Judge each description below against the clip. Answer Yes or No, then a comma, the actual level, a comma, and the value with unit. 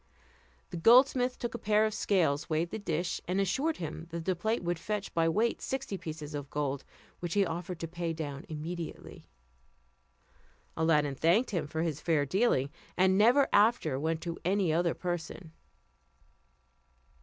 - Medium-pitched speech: Yes, medium, 170 Hz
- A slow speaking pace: No, average, 160 wpm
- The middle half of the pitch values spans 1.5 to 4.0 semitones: No, average, 4.4 semitones